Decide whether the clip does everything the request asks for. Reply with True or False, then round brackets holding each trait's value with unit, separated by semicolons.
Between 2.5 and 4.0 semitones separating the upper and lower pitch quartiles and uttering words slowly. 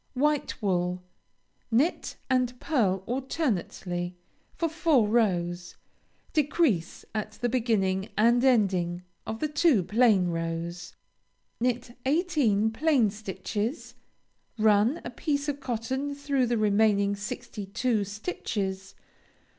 False (5.5 semitones; 105 wpm)